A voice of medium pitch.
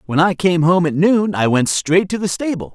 Yes: medium, 180 Hz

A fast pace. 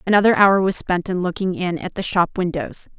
Yes: fast, 220 wpm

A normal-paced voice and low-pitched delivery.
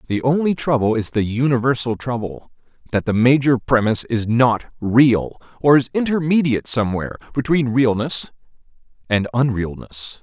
No: slow, 130 wpm; low, 125 Hz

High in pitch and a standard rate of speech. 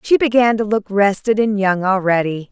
Yes: high, 205 Hz; average, 190 wpm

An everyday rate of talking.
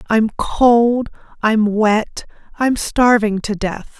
No: slow, 120 wpm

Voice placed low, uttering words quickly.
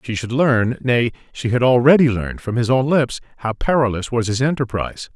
No: low, 125 Hz; average, 175 wpm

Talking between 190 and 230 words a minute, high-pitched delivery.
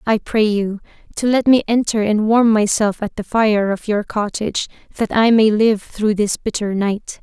Yes: average, 200 wpm; high, 215 Hz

